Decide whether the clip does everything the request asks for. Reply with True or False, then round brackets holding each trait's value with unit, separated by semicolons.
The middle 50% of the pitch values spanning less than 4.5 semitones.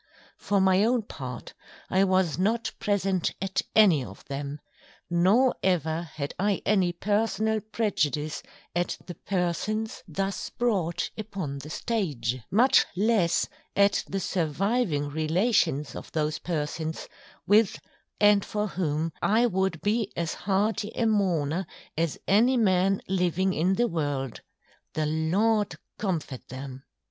False (4.8 semitones)